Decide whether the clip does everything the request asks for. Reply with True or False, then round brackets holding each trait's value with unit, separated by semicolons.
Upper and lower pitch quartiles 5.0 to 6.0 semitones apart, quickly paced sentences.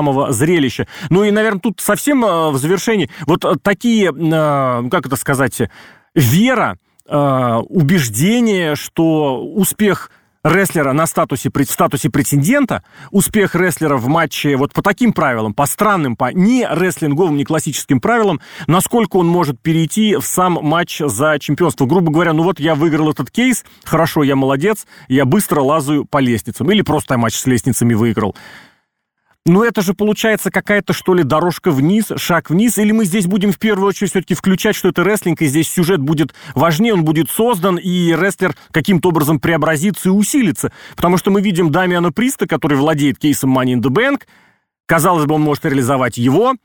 True (5.4 semitones; 165 wpm)